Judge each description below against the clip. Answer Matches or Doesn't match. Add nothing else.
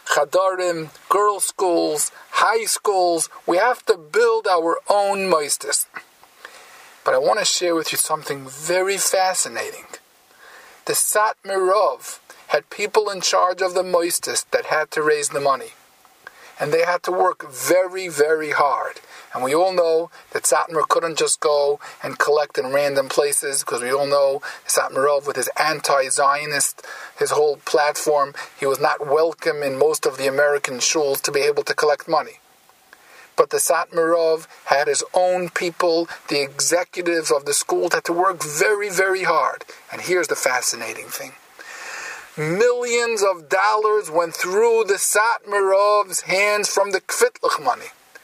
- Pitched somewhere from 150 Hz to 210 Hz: Matches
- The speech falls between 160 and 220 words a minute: Doesn't match